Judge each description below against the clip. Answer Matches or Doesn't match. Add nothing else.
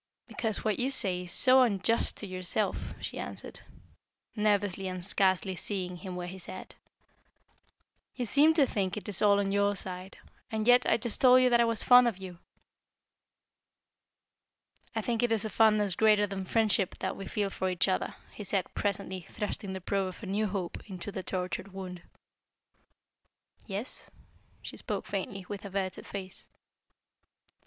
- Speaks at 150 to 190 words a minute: Matches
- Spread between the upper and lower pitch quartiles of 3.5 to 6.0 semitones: Doesn't match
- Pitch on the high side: Matches